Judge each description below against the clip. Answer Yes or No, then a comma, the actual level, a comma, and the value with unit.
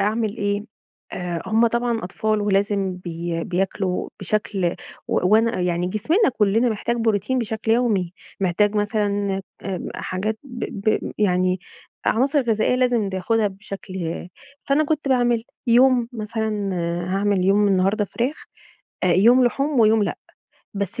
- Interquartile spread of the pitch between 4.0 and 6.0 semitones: No, average, 3.3 semitones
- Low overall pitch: No, high, 210 Hz